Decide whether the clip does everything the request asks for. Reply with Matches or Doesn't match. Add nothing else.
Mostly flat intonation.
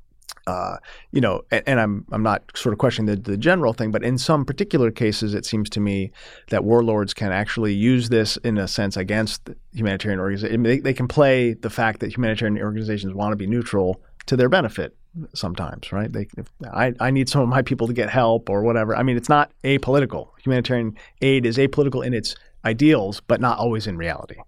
Doesn't match